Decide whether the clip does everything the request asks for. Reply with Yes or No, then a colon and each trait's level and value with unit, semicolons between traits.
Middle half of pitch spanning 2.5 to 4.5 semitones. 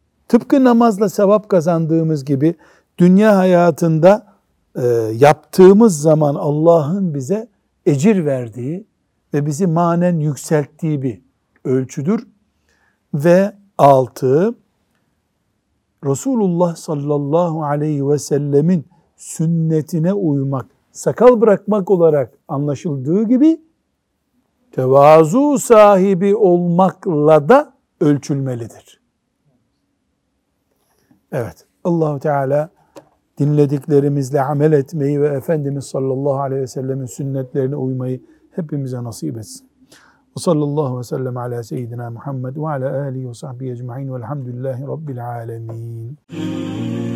No: average, 5.2 semitones